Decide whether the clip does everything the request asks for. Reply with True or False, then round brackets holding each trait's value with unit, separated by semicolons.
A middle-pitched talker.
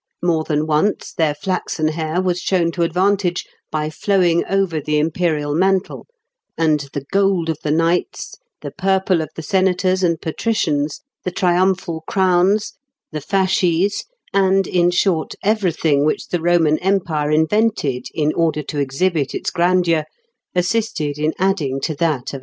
True (170 Hz)